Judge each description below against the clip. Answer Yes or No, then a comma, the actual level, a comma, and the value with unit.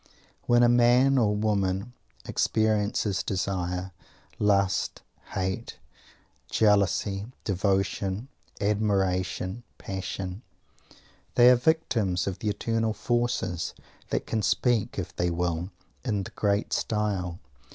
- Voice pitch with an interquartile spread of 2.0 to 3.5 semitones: Yes, average, 3.2 semitones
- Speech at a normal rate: No, slow, 100 wpm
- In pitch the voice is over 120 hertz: No, low, 100 Hz